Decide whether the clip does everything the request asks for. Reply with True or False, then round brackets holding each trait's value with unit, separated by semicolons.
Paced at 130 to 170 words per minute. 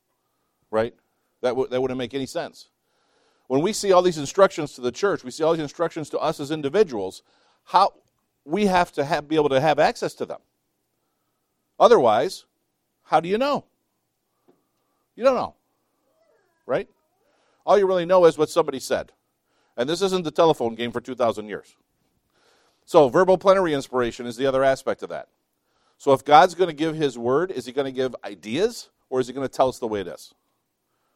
False (190 wpm)